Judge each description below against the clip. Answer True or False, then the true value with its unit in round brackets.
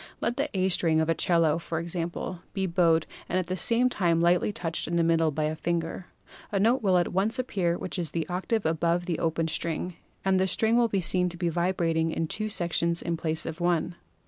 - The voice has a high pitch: False (175 Hz)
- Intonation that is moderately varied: False (2.3 semitones)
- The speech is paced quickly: True (225 wpm)